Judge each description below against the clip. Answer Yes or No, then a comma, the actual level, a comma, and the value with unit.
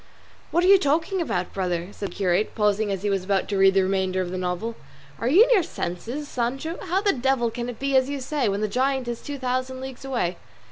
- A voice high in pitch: Yes, high, 240 Hz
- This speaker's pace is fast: Yes, fast, 245 wpm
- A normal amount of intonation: No, wide, 6.1 semitones